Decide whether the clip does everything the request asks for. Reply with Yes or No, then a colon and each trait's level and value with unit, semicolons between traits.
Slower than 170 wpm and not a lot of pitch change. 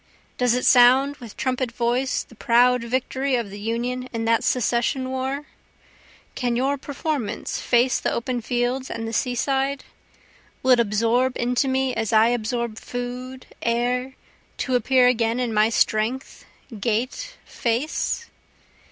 Yes: average, 140 wpm; narrow, 1.9 semitones